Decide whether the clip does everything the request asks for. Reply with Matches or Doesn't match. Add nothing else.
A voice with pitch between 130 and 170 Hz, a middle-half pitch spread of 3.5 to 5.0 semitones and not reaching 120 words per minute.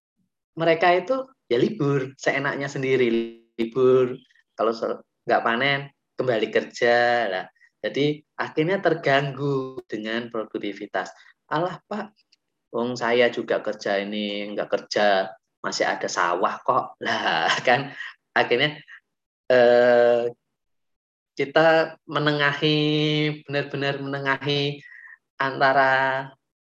Matches